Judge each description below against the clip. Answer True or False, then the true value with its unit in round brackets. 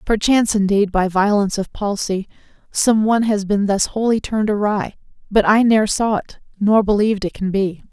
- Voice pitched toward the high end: True (205 Hz)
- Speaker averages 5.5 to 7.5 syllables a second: True (5.6 syllables/s)